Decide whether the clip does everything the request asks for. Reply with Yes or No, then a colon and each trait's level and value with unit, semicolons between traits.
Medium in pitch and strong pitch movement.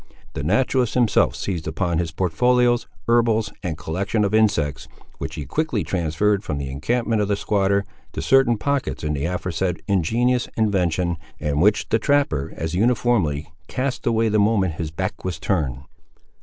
No: low, 100 Hz; wide, 6.2 semitones